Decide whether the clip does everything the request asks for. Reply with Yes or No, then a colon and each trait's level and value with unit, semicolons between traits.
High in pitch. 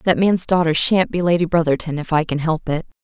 No: medium, 165 Hz